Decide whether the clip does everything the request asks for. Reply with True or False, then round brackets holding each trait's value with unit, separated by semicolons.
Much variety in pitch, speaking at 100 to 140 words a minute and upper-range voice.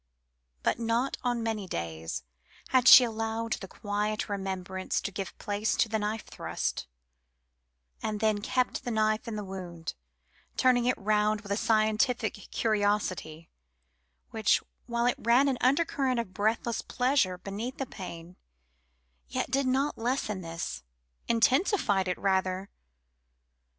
False (3.8 semitones; 135 wpm; 215 Hz)